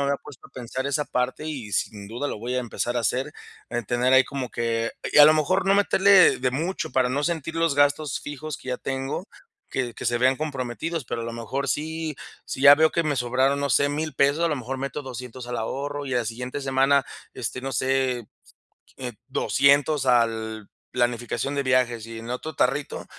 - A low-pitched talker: Yes, low, 130 Hz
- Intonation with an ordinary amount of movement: Yes, average, 3.0 semitones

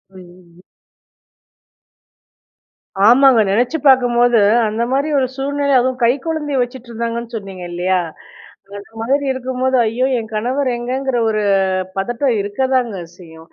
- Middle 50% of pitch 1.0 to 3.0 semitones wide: No, average, 3.6 semitones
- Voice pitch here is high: Yes, high, 240 Hz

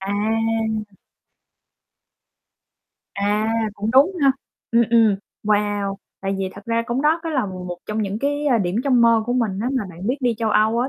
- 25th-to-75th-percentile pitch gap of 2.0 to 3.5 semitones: Yes, average, 3.1 semitones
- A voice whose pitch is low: No, high, 220 Hz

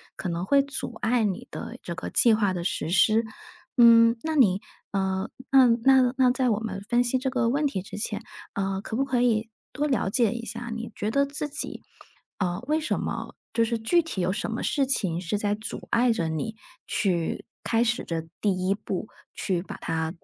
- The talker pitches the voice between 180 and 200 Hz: No, high, 225 Hz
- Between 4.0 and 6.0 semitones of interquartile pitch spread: Yes, average, 4.6 semitones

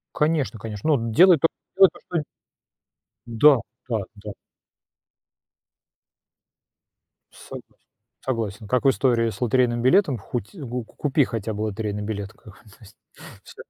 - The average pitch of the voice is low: Yes, low, 120 Hz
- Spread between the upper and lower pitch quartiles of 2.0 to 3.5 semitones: No, average, 4.4 semitones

